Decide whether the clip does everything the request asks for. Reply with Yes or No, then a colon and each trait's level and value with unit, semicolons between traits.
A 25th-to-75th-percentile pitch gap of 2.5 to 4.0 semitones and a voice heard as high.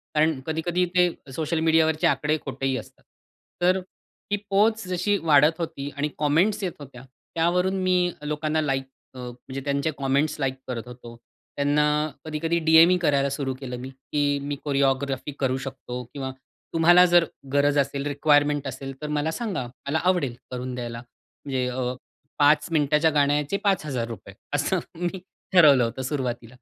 No: average, 3.4 semitones; medium, 145 Hz